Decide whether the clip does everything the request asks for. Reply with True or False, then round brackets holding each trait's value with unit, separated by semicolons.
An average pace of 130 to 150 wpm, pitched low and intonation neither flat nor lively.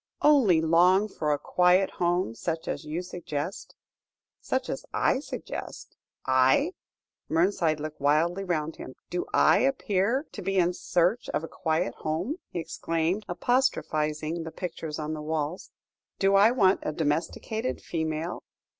False (145 wpm; 170 Hz; 3.7 semitones)